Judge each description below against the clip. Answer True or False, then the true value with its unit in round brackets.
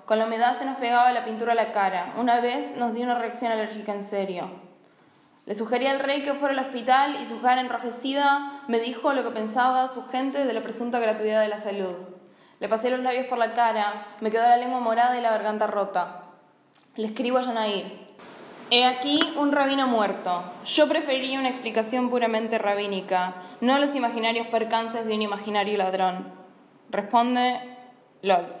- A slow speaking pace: False (185 wpm)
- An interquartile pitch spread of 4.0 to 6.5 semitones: False (3.4 semitones)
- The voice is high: True (230 Hz)